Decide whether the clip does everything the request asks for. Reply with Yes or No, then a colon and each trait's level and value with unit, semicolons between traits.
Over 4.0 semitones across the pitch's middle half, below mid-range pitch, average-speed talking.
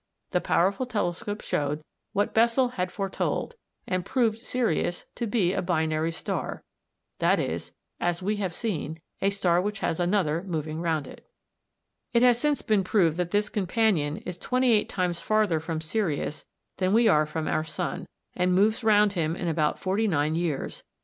No: average, 4.7 semitones; medium, 185 Hz; average, 170 wpm